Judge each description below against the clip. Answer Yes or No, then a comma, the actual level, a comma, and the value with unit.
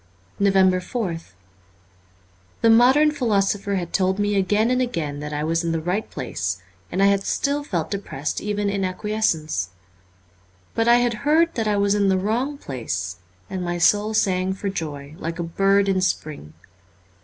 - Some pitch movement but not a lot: Yes, average, 4.4 semitones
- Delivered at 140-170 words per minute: No, average, 180 wpm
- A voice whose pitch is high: Yes, high, 195 Hz